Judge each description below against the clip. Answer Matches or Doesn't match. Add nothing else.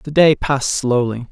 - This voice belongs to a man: Matches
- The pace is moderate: Matches